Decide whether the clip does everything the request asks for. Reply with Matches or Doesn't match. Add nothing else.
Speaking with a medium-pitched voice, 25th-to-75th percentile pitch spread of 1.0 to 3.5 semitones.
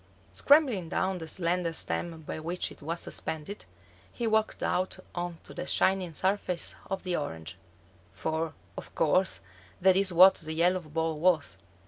Matches